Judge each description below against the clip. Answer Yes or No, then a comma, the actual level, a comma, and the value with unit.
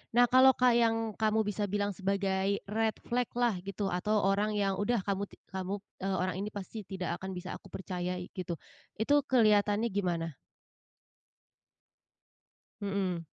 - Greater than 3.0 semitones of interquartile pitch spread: No, narrow, 2.6 semitones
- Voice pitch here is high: Yes, high, 200 Hz